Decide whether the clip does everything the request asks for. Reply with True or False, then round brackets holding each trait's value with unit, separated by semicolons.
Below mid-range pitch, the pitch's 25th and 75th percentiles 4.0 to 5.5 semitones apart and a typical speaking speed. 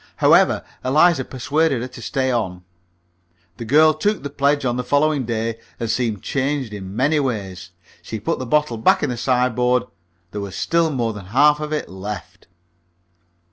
True (125 Hz; 4.6 semitones; 175 wpm)